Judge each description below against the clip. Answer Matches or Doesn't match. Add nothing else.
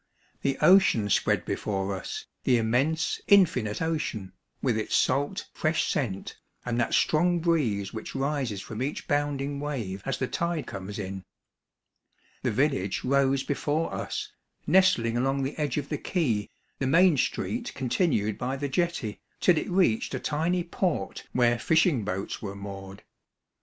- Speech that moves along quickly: Doesn't match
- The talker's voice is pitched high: Doesn't match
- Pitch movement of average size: Doesn't match